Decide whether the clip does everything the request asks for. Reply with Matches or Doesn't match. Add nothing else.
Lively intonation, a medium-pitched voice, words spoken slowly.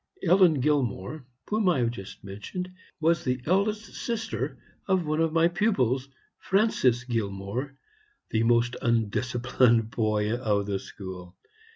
Doesn't match